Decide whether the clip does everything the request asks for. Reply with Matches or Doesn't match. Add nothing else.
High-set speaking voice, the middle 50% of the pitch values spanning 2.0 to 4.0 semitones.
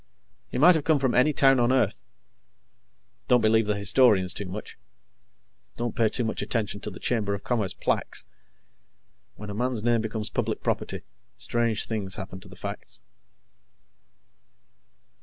Doesn't match